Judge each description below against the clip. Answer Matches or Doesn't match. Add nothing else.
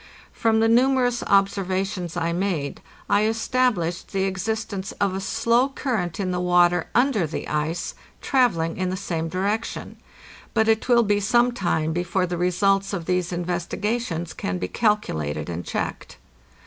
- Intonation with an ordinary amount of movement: Matches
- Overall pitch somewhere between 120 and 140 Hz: Doesn't match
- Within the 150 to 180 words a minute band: Matches